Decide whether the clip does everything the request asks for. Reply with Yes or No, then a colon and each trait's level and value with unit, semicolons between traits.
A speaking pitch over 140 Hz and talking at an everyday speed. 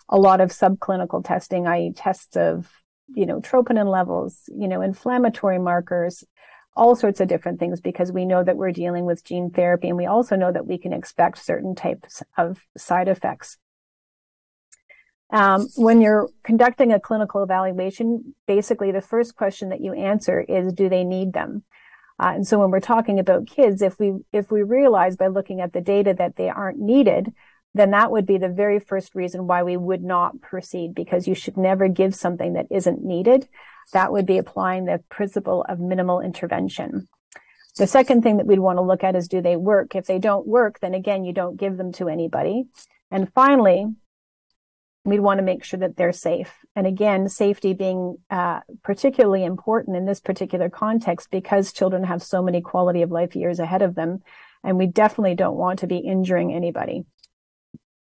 Yes: high, 190 Hz; average, 190 wpm